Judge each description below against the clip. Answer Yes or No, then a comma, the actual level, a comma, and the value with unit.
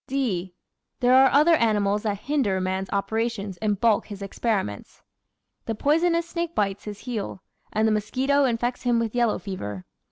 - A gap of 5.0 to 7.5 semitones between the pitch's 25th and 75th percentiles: No, average, 4.5 semitones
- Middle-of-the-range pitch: No, high, 220 Hz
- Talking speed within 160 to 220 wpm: Yes, average, 165 wpm